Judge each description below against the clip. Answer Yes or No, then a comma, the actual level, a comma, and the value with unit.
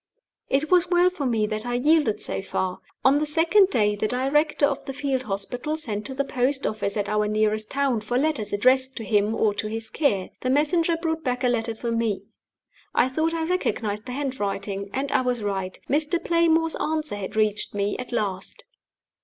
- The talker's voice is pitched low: No, very high, 250 Hz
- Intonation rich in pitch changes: Yes, wide, 6.1 semitones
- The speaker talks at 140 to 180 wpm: No, average, 200 wpm